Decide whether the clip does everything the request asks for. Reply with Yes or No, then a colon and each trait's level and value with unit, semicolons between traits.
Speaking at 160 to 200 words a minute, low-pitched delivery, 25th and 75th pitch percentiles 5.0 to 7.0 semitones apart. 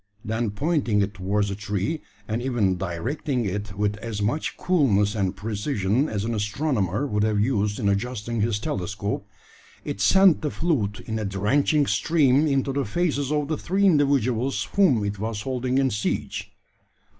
Yes: average, 165 wpm; low, 115 Hz; wide, 5.4 semitones